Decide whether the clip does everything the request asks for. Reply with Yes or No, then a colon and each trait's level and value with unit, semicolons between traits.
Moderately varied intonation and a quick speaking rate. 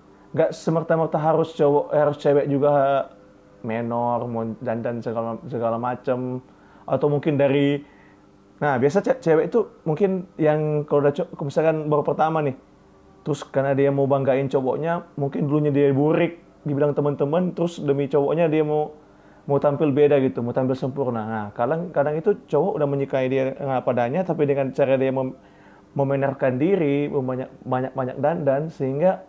Yes: average, 3.0 semitones; fast, 155 wpm